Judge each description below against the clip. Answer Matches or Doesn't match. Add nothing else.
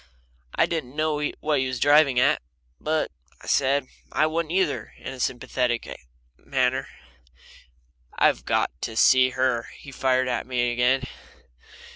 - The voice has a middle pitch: Doesn't match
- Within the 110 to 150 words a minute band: Matches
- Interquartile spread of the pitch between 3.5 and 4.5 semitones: Doesn't match